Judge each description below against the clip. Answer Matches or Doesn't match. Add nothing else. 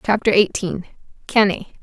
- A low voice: Doesn't match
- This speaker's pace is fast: Doesn't match